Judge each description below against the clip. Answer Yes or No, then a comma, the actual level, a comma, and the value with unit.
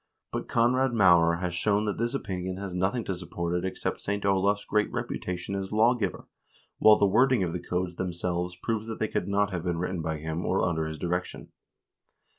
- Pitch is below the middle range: Yes, very low, 95 Hz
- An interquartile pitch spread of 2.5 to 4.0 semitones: Yes, average, 3.2 semitones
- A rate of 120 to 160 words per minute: No, fast, 205 wpm